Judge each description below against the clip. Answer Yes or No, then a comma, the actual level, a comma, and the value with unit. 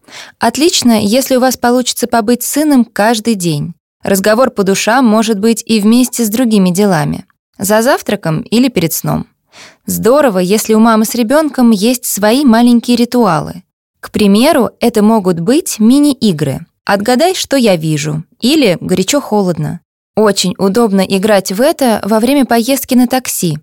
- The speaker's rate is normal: Yes, average, 140 wpm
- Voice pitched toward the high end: Yes, high, 225 Hz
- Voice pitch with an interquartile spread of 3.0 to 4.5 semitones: Yes, average, 3.8 semitones